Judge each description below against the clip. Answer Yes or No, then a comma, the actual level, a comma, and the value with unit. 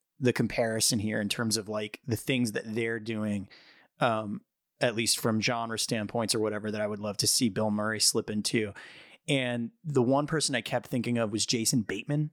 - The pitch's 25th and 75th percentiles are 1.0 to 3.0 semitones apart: Yes, narrow, 2.4 semitones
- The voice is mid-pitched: No, low, 115 Hz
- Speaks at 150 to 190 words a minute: No, average, 200 wpm